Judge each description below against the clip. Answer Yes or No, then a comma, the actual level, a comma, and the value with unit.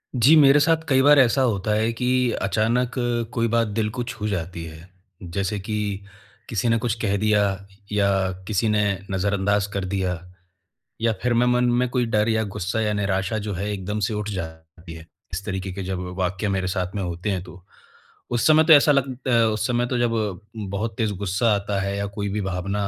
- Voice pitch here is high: No, low, 105 Hz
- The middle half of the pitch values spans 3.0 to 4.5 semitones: Yes, average, 3.6 semitones